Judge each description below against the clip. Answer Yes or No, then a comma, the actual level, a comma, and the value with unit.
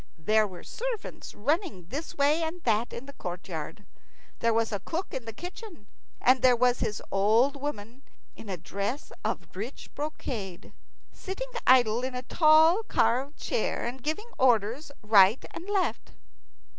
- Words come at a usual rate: Yes, average, 155 wpm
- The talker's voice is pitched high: Yes, very high, 250 Hz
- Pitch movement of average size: No, wide, 6.7 semitones